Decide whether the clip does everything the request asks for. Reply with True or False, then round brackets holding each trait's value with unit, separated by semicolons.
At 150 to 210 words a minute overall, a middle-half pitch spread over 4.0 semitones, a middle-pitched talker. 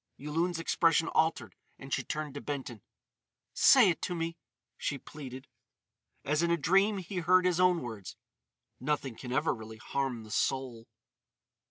True (155 wpm; 4.6 semitones; 150 Hz)